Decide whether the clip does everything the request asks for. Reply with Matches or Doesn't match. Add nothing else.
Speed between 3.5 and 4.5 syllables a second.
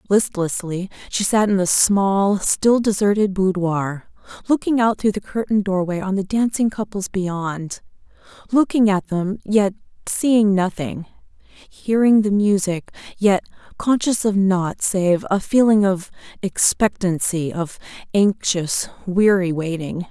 Matches